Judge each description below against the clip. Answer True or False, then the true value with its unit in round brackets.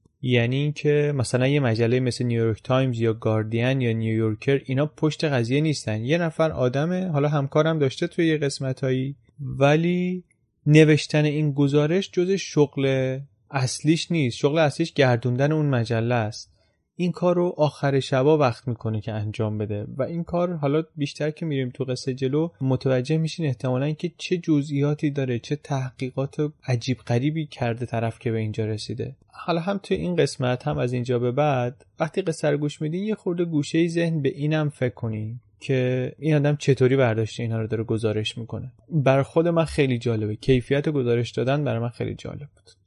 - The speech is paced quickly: True (170 wpm)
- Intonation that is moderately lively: True (4.1 semitones)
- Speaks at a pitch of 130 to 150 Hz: True (135 Hz)